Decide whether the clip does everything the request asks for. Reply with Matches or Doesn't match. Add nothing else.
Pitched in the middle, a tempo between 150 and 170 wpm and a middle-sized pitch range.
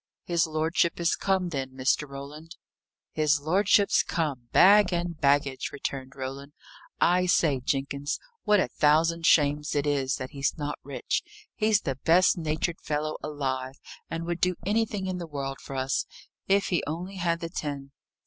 Matches